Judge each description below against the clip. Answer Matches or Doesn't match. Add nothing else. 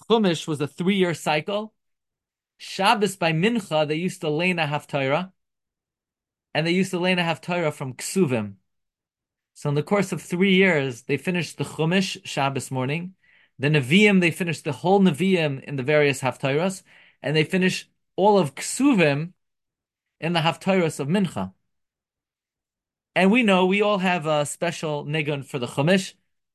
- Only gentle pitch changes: Doesn't match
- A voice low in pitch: Doesn't match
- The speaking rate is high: Doesn't match